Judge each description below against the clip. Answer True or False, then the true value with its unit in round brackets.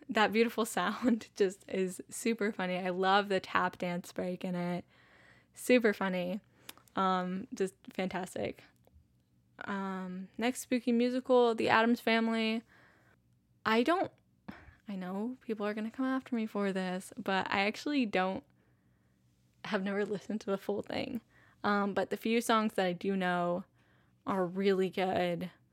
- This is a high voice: True (195 Hz)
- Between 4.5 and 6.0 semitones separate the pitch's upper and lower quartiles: False (3.7 semitones)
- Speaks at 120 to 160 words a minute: True (145 wpm)